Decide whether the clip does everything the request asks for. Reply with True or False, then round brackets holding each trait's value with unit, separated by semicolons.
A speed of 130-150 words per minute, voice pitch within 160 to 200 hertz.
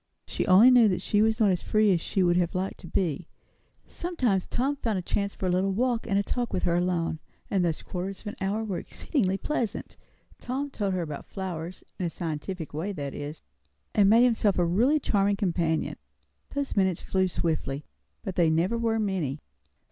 False (200 wpm; 190 Hz)